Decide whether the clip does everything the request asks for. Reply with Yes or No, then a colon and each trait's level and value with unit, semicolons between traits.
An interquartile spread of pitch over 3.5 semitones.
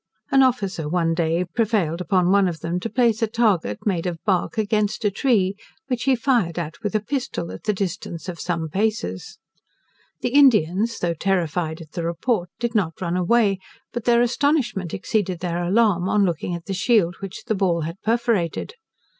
Yes: average, 4.9 semitones